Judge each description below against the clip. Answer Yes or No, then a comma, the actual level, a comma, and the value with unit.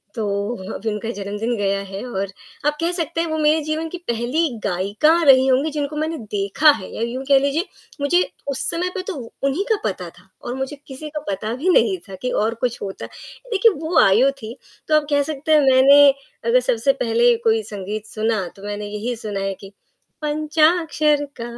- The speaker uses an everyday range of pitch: No, wide, 6.2 semitones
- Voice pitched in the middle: No, very high, 260 Hz